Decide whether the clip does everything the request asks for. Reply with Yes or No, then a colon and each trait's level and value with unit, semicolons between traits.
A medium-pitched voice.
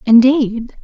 No: high, 245 Hz